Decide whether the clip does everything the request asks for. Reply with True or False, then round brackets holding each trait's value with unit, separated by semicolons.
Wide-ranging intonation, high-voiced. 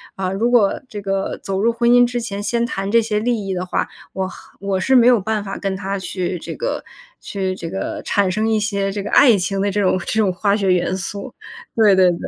False (2.6 semitones; 200 Hz)